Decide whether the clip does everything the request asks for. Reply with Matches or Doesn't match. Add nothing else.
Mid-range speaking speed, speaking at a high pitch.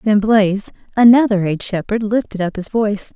Matches